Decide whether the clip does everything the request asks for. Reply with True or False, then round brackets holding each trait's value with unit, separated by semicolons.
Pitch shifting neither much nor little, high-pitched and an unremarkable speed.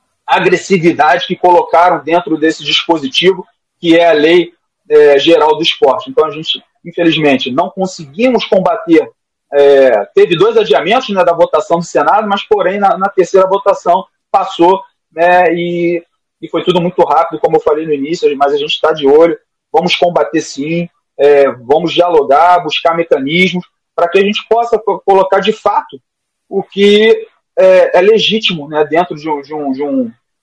False (4.0 semitones; 175 Hz; 165 wpm)